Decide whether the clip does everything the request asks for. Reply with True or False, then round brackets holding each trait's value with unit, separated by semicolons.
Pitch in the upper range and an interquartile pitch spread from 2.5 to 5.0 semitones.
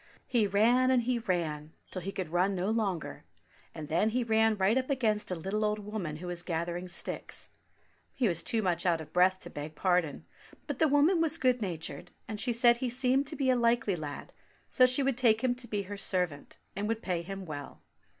False (210 Hz; 5.6 semitones)